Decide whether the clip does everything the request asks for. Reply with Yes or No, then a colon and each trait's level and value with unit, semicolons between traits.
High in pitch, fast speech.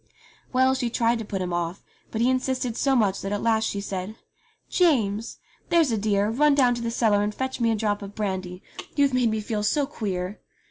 Yes: high, 220 Hz; fast, 220 wpm